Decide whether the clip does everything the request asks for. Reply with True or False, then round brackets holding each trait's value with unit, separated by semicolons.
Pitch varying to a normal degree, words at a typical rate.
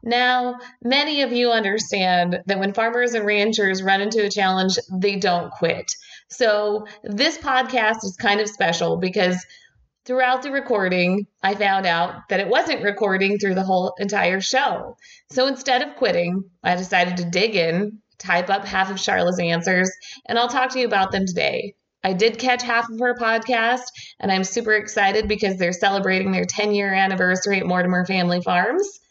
True (4.1 semitones; 175 wpm)